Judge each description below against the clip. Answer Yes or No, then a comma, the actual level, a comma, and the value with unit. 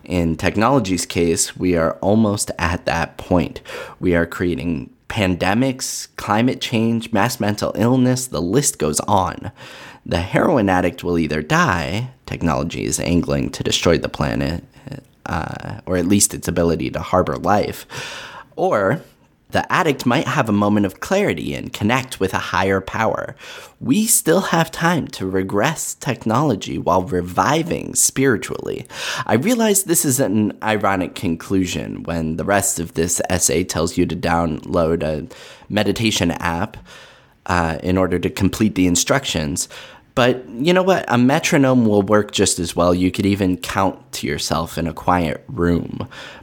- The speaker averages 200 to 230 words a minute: No, average, 150 wpm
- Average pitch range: No, wide, 6.1 semitones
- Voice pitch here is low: Yes, very low, 95 Hz